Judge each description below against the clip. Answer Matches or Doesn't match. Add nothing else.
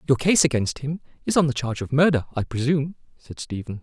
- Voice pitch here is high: Doesn't match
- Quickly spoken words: Matches